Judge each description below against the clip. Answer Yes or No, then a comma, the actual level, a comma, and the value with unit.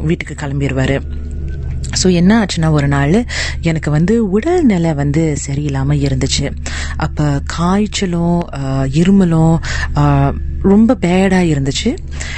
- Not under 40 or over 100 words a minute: Yes, average, 90 wpm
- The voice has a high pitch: No, medium, 145 Hz